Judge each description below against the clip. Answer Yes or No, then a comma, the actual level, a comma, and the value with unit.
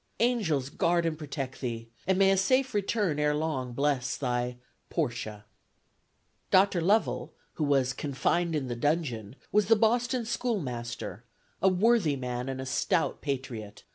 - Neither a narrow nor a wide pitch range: No, wide, 7.3 semitones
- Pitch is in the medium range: Yes, medium, 150 Hz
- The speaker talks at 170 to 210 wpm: No, average, 145 wpm